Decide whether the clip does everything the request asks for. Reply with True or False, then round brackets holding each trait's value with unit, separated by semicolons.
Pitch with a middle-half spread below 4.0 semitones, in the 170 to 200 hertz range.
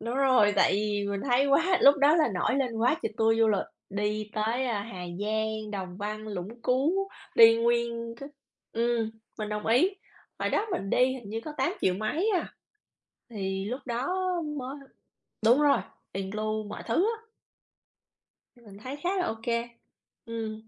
False (3.5 semitones; 230 Hz)